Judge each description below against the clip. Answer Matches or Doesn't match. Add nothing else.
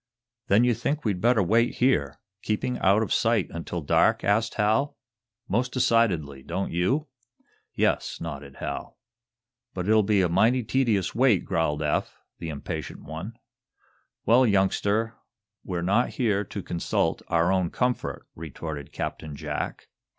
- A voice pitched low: Matches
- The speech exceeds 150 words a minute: Doesn't match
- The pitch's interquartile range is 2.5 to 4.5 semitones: Doesn't match